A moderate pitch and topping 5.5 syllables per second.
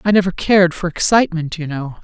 Yes: medium, 175 Hz; 6.3 syllables/s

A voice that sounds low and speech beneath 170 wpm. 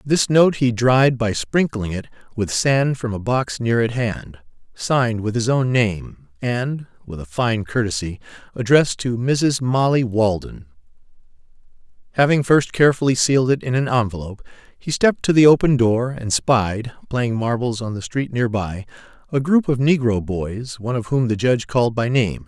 No: low, 120 Hz; average, 175 wpm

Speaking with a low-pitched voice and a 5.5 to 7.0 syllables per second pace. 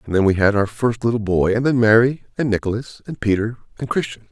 Yes: low, 110 Hz; 6.0 syllables/s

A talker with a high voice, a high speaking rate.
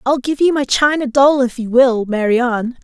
Yes: very high, 255 Hz; fast, 210 wpm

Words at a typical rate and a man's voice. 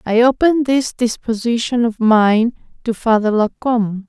No: average, 145 wpm; female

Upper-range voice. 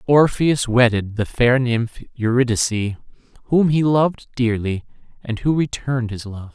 No: low, 125 Hz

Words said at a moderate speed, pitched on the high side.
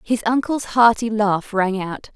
Yes: average, 165 wpm; high, 215 Hz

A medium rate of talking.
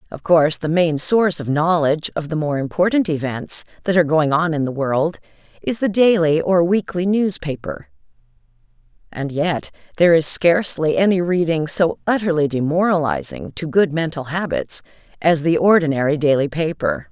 Yes: average, 155 wpm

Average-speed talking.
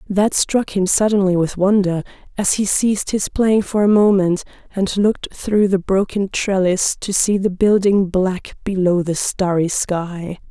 Yes: average, 165 wpm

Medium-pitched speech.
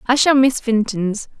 No: high, 235 Hz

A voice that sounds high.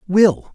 Yes: high, 195 Hz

